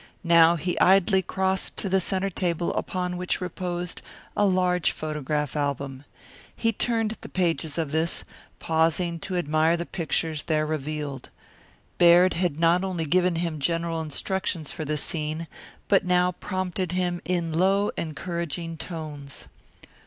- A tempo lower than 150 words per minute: Yes, average, 140 wpm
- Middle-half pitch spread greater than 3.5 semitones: No, average, 2.7 semitones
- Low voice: No, medium, 170 Hz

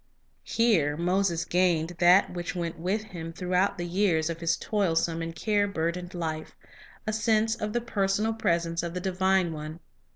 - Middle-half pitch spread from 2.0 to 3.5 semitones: Yes, average, 3.2 semitones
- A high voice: No, medium, 180 Hz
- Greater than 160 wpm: Yes, average, 170 wpm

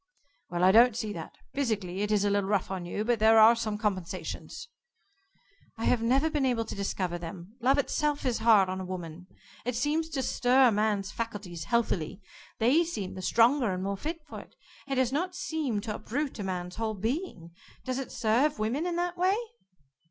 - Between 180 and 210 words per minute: Yes, average, 195 wpm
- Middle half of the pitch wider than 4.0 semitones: Yes, wide, 5.6 semitones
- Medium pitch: No, high, 225 Hz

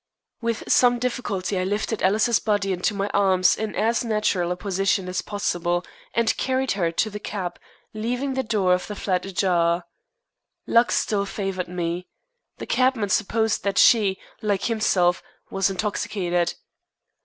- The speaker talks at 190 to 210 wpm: No, average, 150 wpm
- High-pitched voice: Yes, high, 200 Hz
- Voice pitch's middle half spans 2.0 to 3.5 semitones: Yes, average, 3.2 semitones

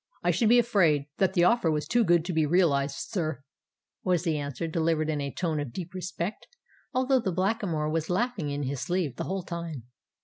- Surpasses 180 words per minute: Yes, fast, 205 wpm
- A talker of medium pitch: Yes, medium, 170 Hz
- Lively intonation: No, average, 3.9 semitones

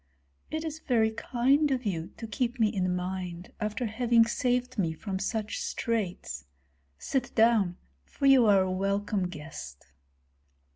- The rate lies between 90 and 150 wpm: Yes, average, 145 wpm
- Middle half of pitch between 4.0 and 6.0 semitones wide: Yes, average, 4.7 semitones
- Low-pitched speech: No, high, 215 Hz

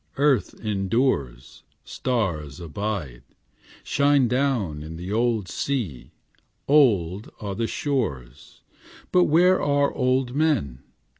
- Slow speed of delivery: Yes, slow, 100 wpm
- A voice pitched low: Yes, low, 110 Hz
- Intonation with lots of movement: Yes, wide, 8.8 semitones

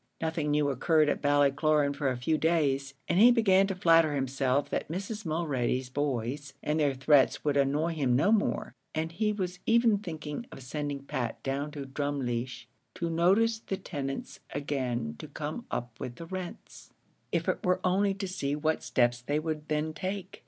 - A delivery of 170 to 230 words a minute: Yes, average, 180 wpm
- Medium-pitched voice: Yes, medium, 150 Hz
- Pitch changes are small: No, average, 4.1 semitones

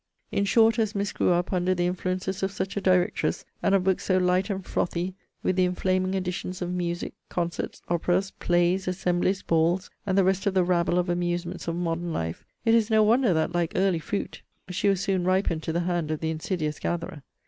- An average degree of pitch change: No, narrow, 1.7 semitones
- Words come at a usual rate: No, fast, 210 wpm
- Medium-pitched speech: Yes, medium, 180 Hz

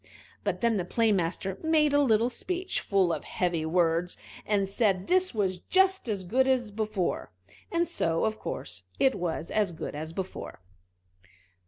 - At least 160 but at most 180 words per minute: Yes, average, 165 wpm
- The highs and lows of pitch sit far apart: Yes, wide, 6.4 semitones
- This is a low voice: No, high, 205 Hz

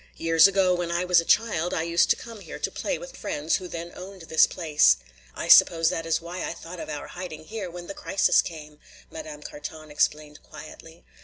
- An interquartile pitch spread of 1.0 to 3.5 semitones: Yes, average, 2.7 semitones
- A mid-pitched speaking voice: Yes, medium, 170 Hz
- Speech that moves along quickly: Yes, fast, 215 wpm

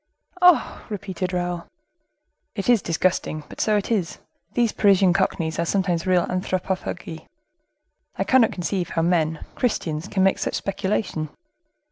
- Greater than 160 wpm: No, slow, 135 wpm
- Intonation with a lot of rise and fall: No, average, 2.9 semitones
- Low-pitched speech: No, medium, 185 Hz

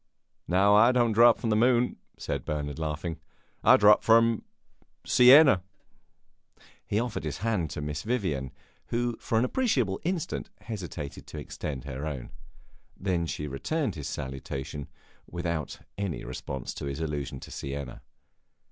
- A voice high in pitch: No, very low, 90 Hz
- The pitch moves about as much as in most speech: No, wide, 7.9 semitones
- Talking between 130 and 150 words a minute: Yes, average, 140 wpm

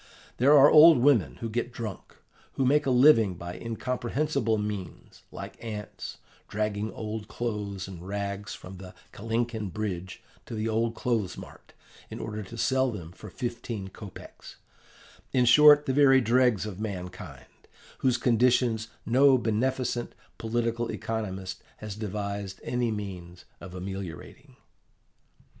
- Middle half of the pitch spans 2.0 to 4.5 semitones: Yes, average, 3.6 semitones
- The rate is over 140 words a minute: No, slow, 135 wpm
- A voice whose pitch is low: Yes, low, 110 Hz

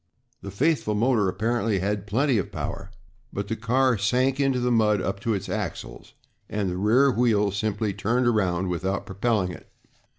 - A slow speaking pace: No, average, 170 wpm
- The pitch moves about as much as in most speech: Yes, average, 3.6 semitones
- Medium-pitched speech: No, low, 105 Hz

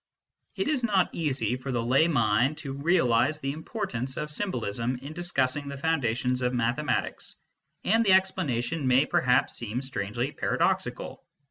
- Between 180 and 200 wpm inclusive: No, average, 150 wpm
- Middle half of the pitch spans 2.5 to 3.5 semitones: No, average, 4.8 semitones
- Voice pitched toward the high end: No, low, 135 Hz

